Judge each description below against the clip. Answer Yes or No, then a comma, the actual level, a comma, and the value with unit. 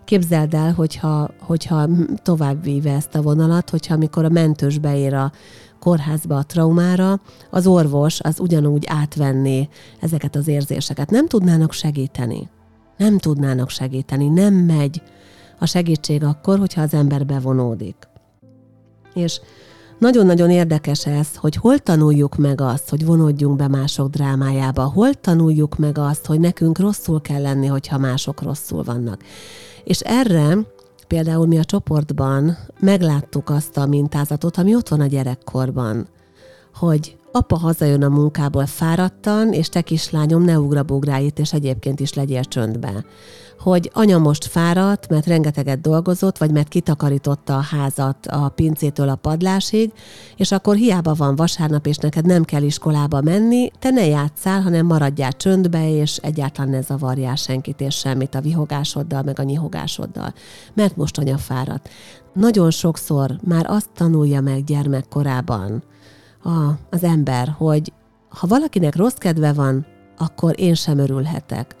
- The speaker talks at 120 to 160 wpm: Yes, average, 140 wpm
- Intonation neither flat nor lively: Yes, average, 3.5 semitones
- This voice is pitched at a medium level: Yes, medium, 150 Hz